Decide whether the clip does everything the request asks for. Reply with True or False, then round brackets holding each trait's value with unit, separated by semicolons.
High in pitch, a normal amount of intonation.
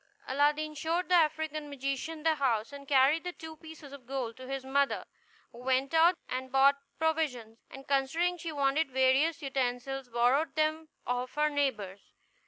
True (280 Hz; 3.2 semitones)